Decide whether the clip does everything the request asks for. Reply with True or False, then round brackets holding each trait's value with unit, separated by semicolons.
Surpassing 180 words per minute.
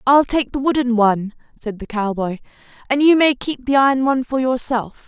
True (200 wpm)